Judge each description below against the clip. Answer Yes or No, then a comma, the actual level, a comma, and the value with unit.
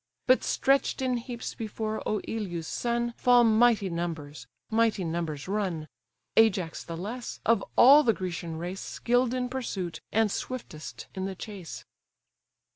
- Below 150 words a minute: Yes, slow, 135 wpm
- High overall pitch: Yes, high, 210 Hz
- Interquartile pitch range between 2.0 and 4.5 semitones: No, wide, 5.6 semitones